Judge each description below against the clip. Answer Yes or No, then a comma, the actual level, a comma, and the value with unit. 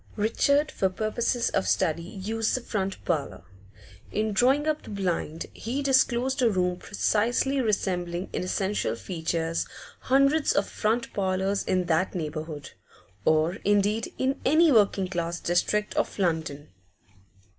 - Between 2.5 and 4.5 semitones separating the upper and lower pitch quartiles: No, wide, 5.4 semitones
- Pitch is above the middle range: Yes, high, 195 Hz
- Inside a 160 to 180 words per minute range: No, slow, 135 wpm